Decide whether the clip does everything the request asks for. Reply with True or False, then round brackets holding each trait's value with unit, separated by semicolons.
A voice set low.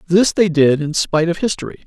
False (175 Hz)